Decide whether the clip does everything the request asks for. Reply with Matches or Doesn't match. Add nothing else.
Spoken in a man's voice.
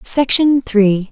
Doesn't match